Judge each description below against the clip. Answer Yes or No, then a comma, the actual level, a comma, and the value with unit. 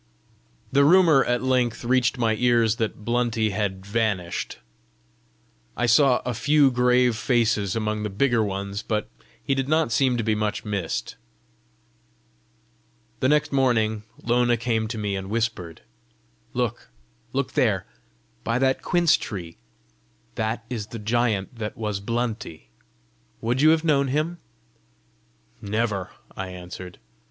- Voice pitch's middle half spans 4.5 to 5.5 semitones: No, average, 3.0 semitones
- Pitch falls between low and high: No, low, 115 Hz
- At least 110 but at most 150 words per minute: Yes, slow, 135 wpm